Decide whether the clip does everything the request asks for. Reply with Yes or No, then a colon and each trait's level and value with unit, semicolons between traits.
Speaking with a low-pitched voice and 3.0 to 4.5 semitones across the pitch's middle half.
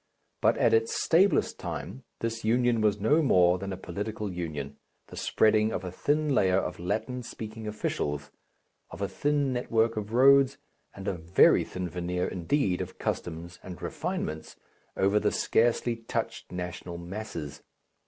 No: low, 105 Hz; average, 5.0 semitones